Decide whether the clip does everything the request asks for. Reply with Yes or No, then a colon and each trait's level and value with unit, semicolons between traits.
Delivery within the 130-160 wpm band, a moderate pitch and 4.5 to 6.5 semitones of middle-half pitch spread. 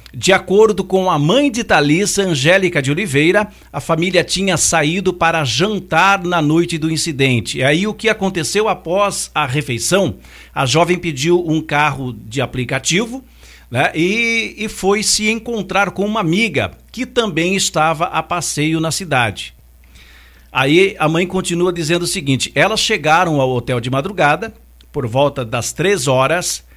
Yes: average, 155 wpm; medium, 170 Hz; average, 5.3 semitones